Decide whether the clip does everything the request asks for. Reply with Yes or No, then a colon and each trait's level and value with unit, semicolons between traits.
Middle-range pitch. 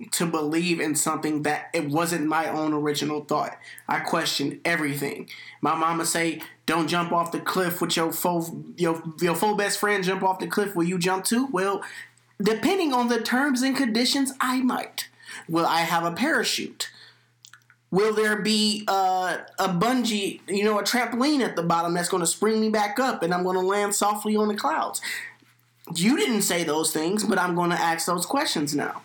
Yes: medium, 180 Hz